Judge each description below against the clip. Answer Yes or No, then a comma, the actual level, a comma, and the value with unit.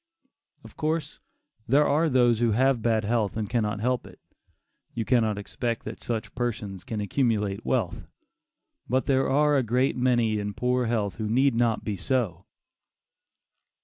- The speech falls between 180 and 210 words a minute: No, average, 155 wpm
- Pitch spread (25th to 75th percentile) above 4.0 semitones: No, average, 3.2 semitones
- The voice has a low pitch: Yes, low, 115 Hz